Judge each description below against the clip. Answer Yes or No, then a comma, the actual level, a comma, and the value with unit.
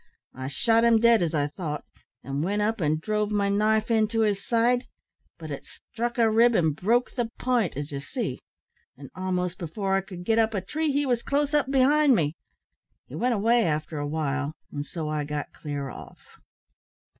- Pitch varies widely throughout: Yes, wide, 7.2 semitones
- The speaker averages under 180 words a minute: No, average, 195 wpm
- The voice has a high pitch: Yes, high, 205 Hz